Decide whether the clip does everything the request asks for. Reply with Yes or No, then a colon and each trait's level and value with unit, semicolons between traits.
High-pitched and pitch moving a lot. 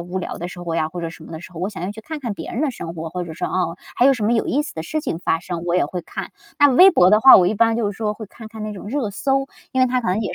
Yes: high, 205 Hz; wide, 5.9 semitones